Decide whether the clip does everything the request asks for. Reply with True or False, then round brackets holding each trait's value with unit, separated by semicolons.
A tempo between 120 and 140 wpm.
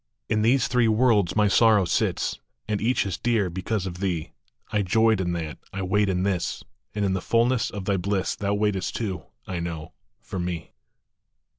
False (185 wpm)